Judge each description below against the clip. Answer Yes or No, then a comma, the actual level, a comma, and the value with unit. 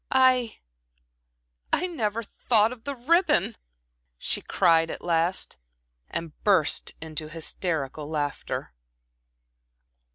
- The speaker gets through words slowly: Yes, slow, 95 wpm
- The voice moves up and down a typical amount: No, wide, 7.2 semitones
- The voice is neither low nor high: Yes, medium, 180 Hz